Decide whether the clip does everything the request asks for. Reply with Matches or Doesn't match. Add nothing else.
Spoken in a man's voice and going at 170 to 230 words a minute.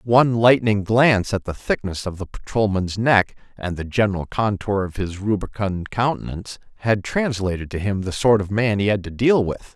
Matches